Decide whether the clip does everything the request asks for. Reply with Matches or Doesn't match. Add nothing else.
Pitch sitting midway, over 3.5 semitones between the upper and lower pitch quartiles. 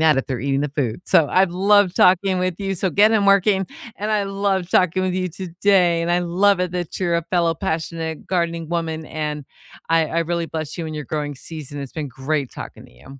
Doesn't match